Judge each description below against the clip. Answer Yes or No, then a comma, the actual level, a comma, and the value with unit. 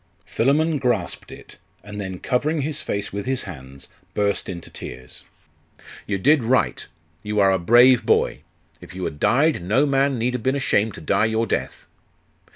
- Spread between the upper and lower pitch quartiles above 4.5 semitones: Yes, wide, 5.5 semitones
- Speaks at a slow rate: No, average, 170 wpm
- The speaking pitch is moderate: No, low, 110 Hz